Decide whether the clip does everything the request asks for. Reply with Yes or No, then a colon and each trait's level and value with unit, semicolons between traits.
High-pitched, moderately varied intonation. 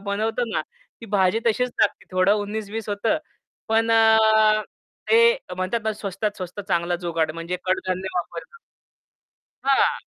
Yes: high, 205 Hz; average, 3.6 semitones